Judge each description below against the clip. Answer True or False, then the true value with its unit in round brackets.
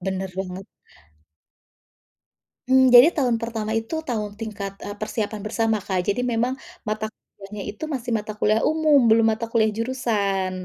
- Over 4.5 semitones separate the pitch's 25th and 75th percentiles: False (2.8 semitones)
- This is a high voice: True (220 Hz)